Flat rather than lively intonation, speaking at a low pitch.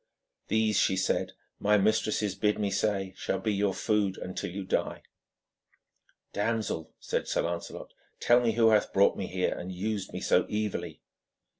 Yes: narrow, 2.2 semitones; low, 105 Hz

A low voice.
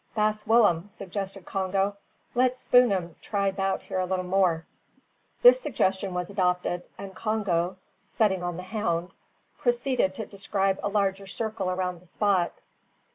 No: high, 195 Hz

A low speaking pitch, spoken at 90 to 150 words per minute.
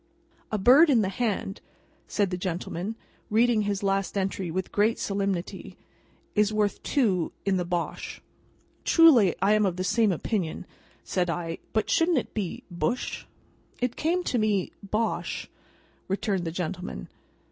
No: high, 200 Hz; average, 145 wpm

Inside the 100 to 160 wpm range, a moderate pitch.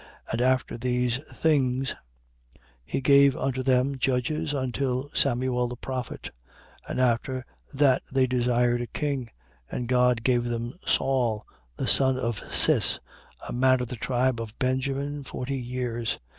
No: average, 145 wpm; low, 130 Hz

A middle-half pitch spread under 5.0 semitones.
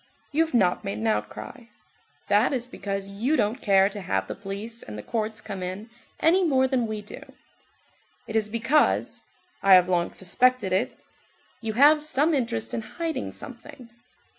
No: average, 5.3 semitones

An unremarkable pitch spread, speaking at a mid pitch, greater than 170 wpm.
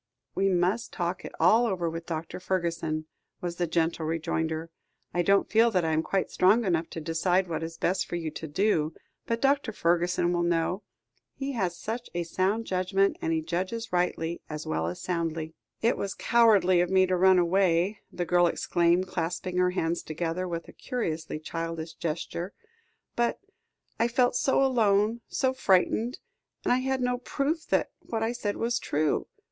Yes: average, 4.6 semitones; medium, 180 Hz; average, 180 wpm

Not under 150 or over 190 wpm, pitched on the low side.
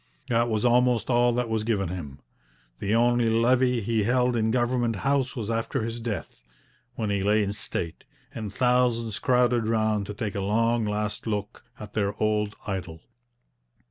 Yes: average, 170 wpm; low, 115 Hz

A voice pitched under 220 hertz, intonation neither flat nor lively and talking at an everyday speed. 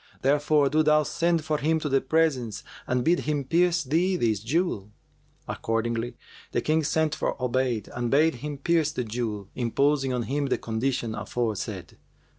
Yes: low, 135 Hz; average, 4.6 semitones; average, 165 wpm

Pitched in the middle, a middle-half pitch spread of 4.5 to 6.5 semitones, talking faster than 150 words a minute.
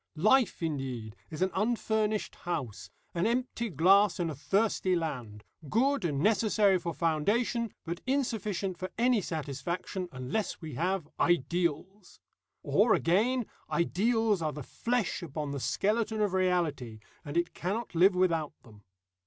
No: medium, 180 Hz; wide, 5.6 semitones; slow, 135 wpm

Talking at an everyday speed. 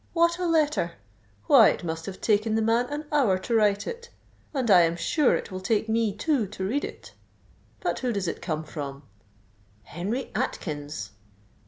Yes: average, 180 wpm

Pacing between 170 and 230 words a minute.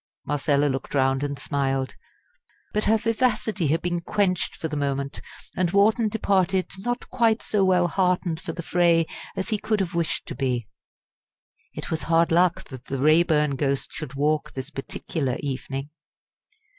No: average, 160 wpm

